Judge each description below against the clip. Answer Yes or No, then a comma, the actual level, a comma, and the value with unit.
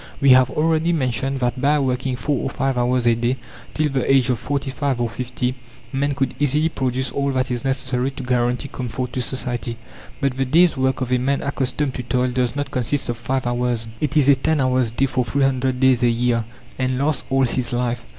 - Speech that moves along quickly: Yes, fast, 220 wpm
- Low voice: Yes, low, 130 Hz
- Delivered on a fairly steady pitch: Yes, narrow, 1.8 semitones